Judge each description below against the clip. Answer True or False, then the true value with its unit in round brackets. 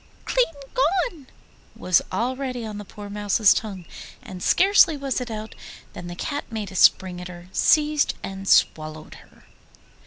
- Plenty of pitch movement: True (6.9 semitones)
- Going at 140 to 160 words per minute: True (155 wpm)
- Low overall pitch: False (215 Hz)